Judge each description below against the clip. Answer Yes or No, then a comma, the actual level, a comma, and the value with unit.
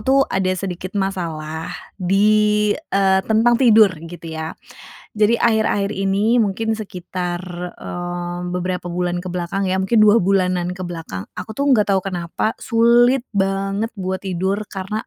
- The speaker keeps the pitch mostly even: No, average, 3.2 semitones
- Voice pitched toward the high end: Yes, high, 195 Hz